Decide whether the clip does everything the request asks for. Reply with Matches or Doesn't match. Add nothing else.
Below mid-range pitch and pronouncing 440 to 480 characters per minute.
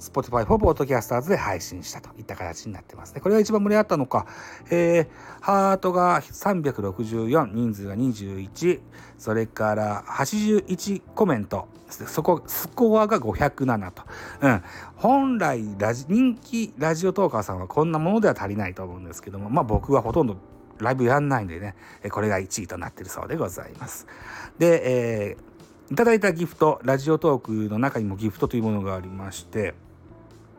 Doesn't match